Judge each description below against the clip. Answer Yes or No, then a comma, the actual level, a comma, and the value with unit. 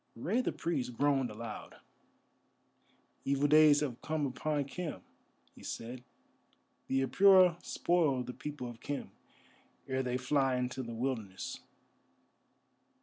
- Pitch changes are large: No, average, 3.4 semitones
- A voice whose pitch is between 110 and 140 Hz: Yes, low, 135 Hz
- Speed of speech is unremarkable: No, slow, 120 wpm